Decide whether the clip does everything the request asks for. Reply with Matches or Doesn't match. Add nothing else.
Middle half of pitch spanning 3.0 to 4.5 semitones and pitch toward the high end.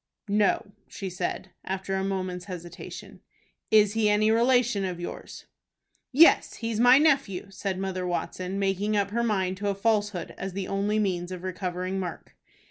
Doesn't match